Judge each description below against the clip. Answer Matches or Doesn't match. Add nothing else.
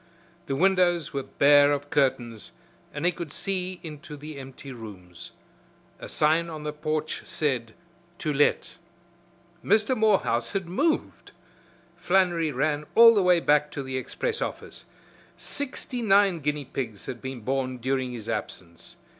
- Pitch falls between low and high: Matches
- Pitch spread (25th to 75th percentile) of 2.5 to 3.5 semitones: Doesn't match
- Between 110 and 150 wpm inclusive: Matches